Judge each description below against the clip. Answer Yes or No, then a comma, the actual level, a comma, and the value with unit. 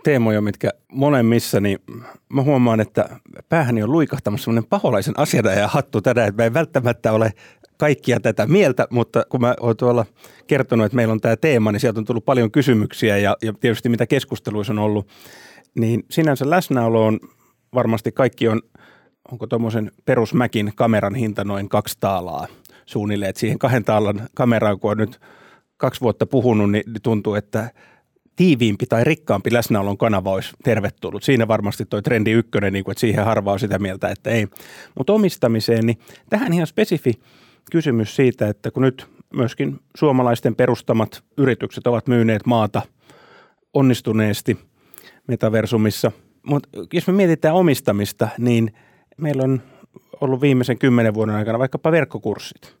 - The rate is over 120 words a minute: Yes, average, 150 wpm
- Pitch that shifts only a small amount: No, average, 3.5 semitones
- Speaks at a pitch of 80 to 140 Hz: Yes, low, 115 Hz